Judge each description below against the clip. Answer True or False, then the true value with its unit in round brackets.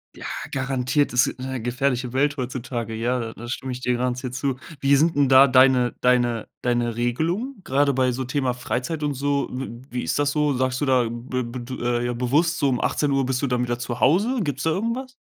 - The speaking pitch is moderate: False (130 Hz)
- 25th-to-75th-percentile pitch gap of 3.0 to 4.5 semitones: False (2.5 semitones)